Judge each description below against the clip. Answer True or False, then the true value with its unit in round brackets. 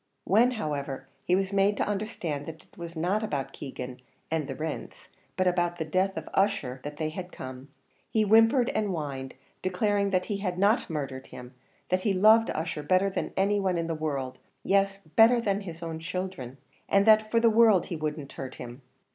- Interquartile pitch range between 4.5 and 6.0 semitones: True (5.0 semitones)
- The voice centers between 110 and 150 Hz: False (180 Hz)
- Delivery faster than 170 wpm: True (200 wpm)